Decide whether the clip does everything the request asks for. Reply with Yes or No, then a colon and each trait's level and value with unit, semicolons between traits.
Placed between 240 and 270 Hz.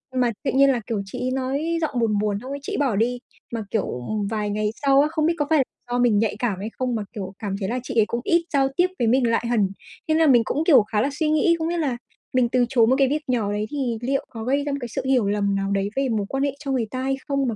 Yes: very high, 250 Hz